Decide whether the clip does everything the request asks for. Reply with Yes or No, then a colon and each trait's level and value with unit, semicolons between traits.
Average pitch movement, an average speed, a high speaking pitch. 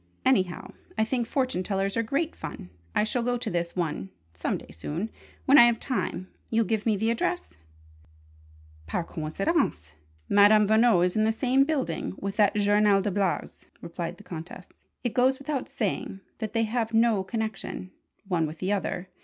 Yes: average, 4.3 semitones; average, 175 wpm; high, 210 Hz